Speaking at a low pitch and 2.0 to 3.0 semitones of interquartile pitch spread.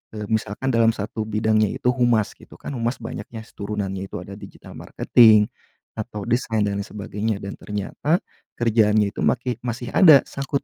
Yes: low, 110 Hz; narrow, 2.5 semitones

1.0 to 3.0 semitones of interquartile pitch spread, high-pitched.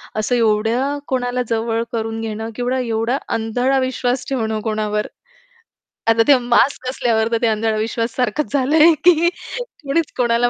Yes: narrow, 2.6 semitones; high, 240 Hz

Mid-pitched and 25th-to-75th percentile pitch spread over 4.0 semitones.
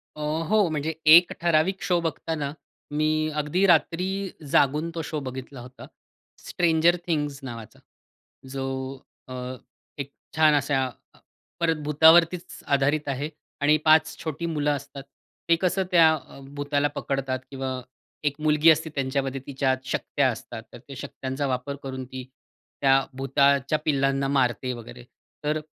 No: medium, 145 Hz; average, 2.9 semitones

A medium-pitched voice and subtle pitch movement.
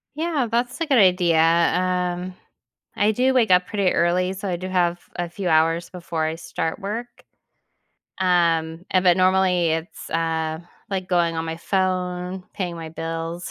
Yes: medium, 180 Hz; narrow, 2.2 semitones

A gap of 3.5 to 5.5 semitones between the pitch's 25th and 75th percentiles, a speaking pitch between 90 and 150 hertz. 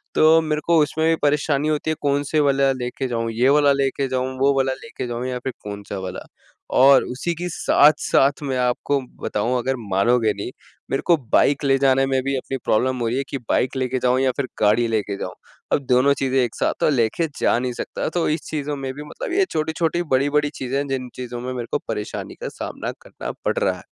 No: narrow, 2.6 semitones; low, 135 Hz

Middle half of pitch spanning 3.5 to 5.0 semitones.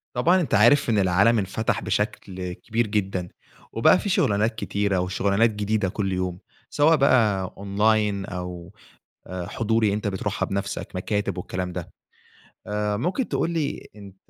No: average, 3.1 semitones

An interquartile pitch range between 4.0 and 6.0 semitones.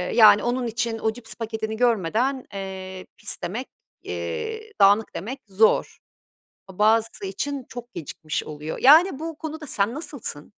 Yes: average, 5.1 semitones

